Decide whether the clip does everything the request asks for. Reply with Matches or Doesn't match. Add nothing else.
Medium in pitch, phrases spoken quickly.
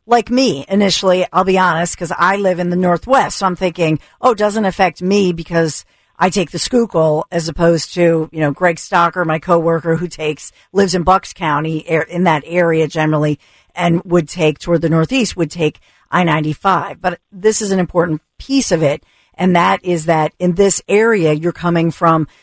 Doesn't match